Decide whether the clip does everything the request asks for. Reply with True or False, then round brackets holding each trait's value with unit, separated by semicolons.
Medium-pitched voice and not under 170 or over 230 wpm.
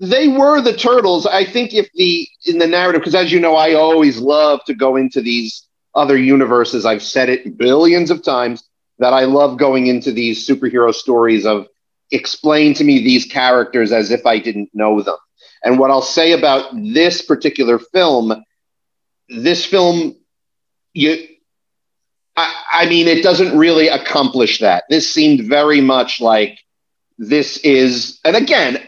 False (150 Hz; 160 wpm)